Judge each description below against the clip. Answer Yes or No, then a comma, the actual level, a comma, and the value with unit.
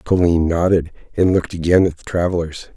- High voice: No, very low, 85 Hz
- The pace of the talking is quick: No, average, 175 wpm